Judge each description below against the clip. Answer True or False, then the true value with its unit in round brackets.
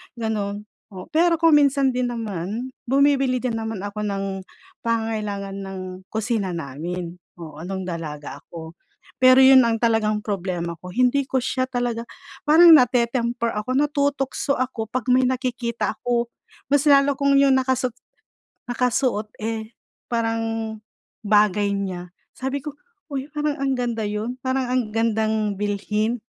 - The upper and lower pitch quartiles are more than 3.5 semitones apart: True (3.9 semitones)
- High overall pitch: True (230 Hz)